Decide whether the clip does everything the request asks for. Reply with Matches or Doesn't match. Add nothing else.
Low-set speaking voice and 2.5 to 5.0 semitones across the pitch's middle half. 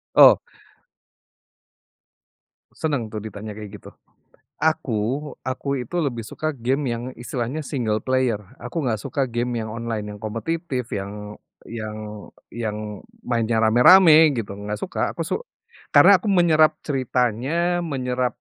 Doesn't match